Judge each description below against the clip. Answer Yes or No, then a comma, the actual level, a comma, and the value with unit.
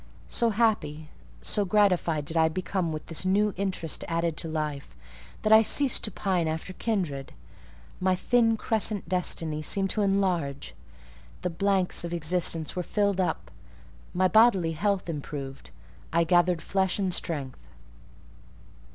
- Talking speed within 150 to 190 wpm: No, average, 140 wpm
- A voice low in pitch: No, medium, 180 Hz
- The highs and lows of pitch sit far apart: No, average, 3.8 semitones